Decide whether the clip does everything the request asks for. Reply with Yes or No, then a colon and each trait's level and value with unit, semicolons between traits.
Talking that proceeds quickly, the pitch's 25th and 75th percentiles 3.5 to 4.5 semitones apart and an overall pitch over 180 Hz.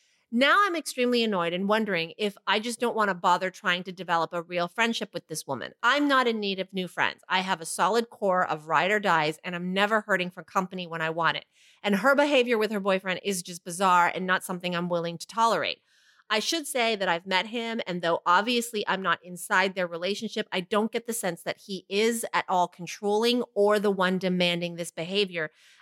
Yes: fast, 225 wpm; average, 3.9 semitones; high, 190 Hz